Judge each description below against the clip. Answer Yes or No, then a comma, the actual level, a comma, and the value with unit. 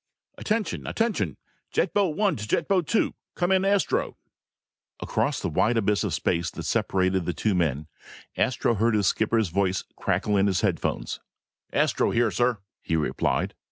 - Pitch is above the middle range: No, low, 110 Hz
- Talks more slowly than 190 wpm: Yes, average, 160 wpm